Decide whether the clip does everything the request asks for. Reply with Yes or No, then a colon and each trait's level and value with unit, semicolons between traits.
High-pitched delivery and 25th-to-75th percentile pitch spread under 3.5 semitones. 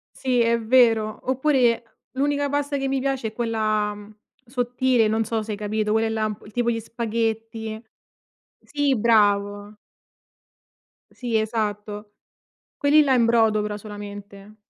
Yes: high, 225 Hz; narrow, 2.6 semitones